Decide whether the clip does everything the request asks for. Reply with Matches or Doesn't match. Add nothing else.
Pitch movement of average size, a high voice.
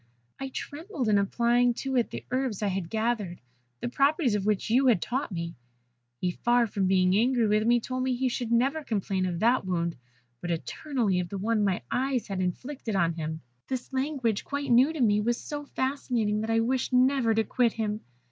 Matches